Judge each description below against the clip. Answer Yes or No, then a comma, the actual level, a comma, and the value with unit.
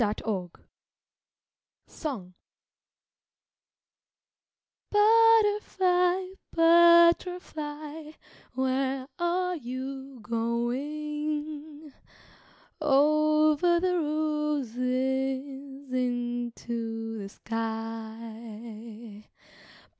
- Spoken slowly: Yes, slow, 40 wpm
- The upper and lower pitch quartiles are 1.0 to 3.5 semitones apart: No, average, 4.9 semitones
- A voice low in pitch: No, very high, 275 Hz